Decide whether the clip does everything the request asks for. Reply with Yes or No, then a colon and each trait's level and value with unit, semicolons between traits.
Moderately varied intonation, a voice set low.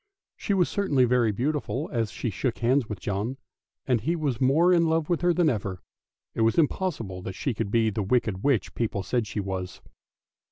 No: wide, 6.3 semitones; low, 120 Hz